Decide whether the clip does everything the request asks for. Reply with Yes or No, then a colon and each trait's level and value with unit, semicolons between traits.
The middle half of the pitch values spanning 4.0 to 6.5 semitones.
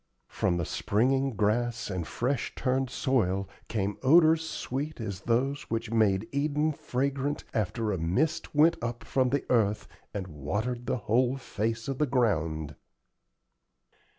Yes: average, 4.8 semitones